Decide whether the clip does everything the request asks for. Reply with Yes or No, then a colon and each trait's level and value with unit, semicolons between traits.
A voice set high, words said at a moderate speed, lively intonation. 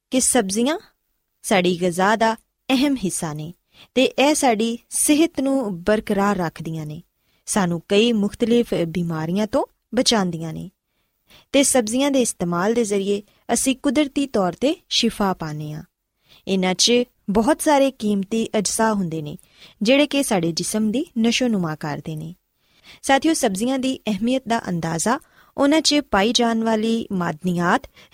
Yes: high, 220 Hz; average, 135 wpm; wide, 6.1 semitones